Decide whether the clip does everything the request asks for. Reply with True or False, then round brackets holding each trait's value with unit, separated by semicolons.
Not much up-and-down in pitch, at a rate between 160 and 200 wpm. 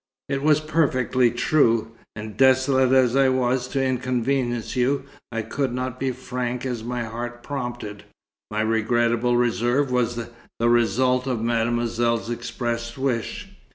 False (1.8 semitones; 140 wpm)